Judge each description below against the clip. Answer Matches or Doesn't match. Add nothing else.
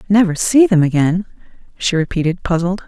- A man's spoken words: Doesn't match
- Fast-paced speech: Doesn't match